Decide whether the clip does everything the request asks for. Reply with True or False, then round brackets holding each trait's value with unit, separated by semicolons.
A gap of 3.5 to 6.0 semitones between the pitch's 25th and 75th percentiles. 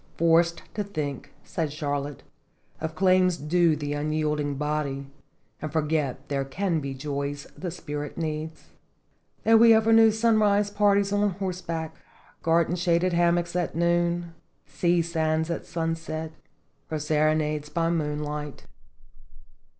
False (2.8 semitones)